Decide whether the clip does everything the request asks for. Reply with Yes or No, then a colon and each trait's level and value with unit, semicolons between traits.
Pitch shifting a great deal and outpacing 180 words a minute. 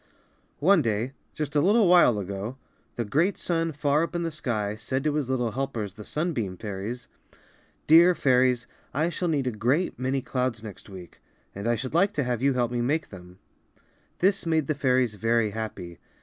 Yes: wide, 5.8 semitones; average, 190 wpm